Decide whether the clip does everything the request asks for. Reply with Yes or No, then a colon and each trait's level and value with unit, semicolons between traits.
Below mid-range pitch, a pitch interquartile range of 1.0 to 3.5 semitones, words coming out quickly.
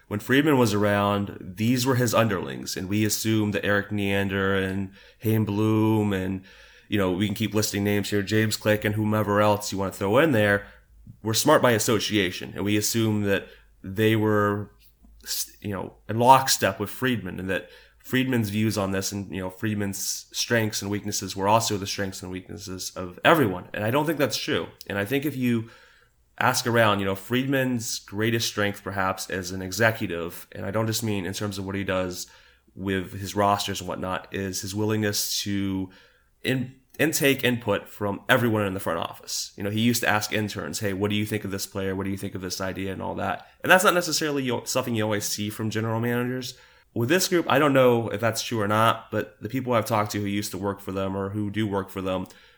Yes: low, 105 Hz; narrow, 2.4 semitones; fast, 215 wpm